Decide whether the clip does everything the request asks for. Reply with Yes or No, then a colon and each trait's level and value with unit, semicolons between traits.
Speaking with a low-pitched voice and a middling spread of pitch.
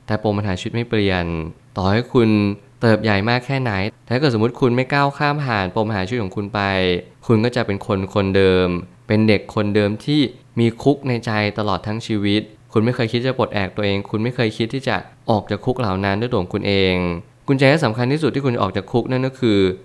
Yes: low, 110 Hz; average, 3.6 semitones